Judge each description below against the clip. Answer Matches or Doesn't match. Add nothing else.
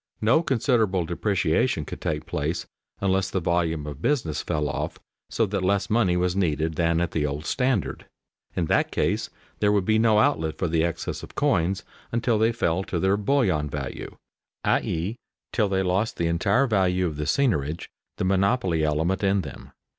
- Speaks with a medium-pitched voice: Doesn't match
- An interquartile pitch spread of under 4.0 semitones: Doesn't match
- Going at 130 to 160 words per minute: Doesn't match